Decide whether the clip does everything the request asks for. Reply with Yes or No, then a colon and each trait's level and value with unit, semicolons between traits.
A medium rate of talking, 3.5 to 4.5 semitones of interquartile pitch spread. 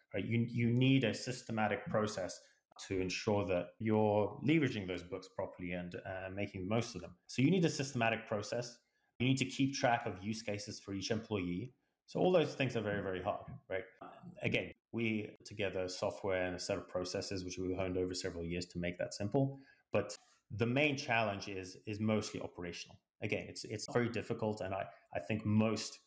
Yes: average, 195 wpm; average, 4.0 semitones